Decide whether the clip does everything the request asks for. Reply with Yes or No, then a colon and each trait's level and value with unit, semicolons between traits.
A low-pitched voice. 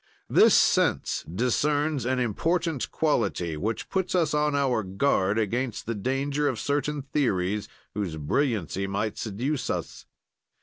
Yes: low, 125 Hz